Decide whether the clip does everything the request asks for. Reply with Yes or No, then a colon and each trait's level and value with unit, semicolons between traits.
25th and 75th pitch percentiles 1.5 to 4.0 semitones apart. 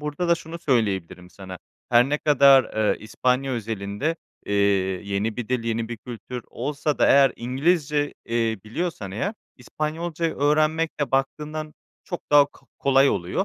No: average, 5.2 semitones